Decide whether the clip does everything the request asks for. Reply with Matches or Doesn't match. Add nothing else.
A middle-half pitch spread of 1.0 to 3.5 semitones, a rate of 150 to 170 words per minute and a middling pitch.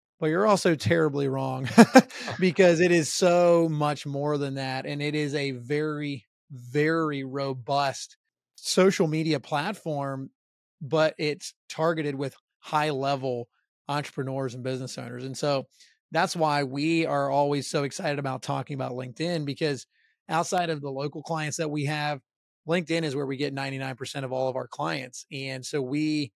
Matches